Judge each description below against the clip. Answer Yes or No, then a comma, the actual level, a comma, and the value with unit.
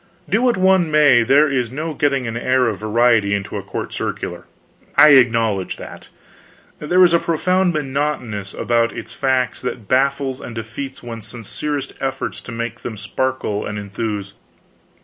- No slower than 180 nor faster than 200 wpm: No, average, 160 wpm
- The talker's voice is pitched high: No, low, 125 Hz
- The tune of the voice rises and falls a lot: No, average, 4.5 semitones